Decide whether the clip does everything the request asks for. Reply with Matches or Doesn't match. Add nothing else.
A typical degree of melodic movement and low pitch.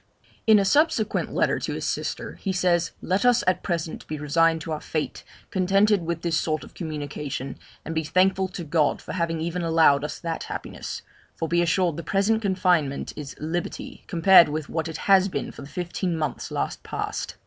Doesn't match